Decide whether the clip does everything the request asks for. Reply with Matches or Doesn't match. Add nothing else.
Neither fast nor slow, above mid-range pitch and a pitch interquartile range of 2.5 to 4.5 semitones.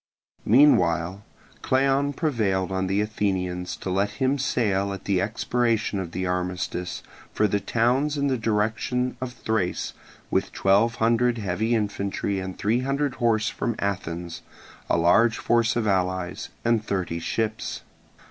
Doesn't match